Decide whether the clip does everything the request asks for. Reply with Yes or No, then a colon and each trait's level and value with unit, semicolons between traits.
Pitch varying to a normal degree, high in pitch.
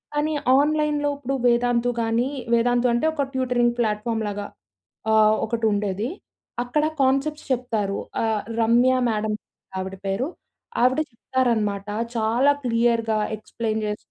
Yes: average, 3.1 semitones; high, 235 Hz